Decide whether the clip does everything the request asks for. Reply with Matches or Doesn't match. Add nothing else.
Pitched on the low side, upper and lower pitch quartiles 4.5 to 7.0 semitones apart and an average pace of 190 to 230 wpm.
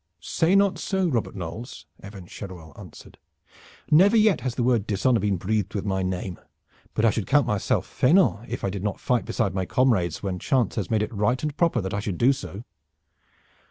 Matches